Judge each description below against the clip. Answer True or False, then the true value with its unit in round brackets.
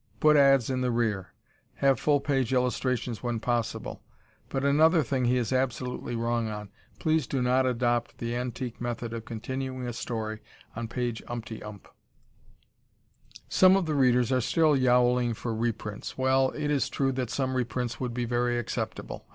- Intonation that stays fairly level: True (2.0 semitones)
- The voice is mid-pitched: False (125 Hz)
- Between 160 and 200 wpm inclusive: True (165 wpm)